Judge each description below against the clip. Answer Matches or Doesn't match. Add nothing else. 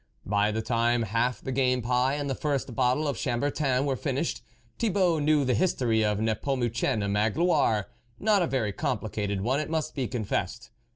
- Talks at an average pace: Matches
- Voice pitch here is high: Doesn't match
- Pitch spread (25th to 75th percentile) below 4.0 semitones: Doesn't match